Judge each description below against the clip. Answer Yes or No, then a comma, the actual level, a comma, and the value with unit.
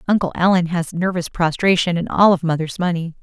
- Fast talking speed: No, average, 185 wpm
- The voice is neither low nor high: Yes, medium, 175 Hz